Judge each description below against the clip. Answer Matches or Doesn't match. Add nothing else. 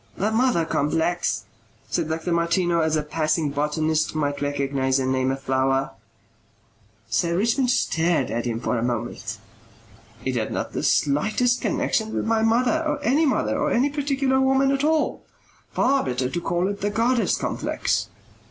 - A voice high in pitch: Doesn't match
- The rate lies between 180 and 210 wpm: Doesn't match